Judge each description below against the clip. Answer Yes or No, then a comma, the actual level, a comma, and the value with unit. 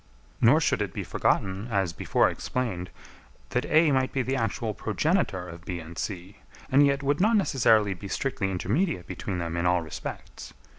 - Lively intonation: Yes, wide, 7.2 semitones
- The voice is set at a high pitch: No, low, 105 Hz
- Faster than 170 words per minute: Yes, average, 180 wpm